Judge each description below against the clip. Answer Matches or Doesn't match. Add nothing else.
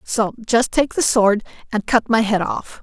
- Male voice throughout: Doesn't match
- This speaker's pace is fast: Matches